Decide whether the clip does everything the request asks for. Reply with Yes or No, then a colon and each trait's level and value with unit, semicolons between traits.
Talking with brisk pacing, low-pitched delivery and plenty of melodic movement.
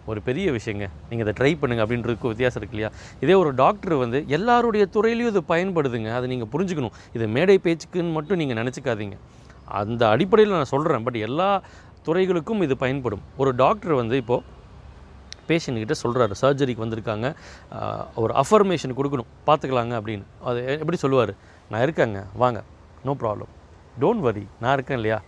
Yes: fast, 150 wpm; low, 125 Hz; wide, 6.1 semitones